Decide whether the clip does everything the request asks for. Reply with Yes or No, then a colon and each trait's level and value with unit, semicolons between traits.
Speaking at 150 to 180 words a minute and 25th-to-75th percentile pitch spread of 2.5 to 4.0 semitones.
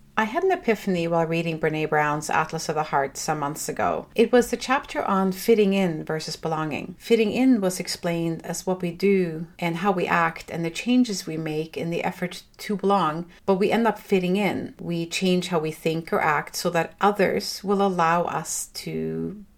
No: average, 200 wpm; average, 3.7 semitones